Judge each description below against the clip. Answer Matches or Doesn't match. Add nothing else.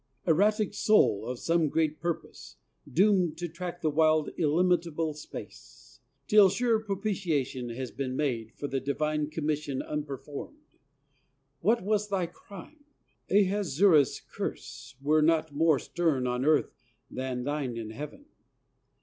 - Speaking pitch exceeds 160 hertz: Doesn't match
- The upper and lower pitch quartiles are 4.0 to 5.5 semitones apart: Matches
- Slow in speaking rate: Matches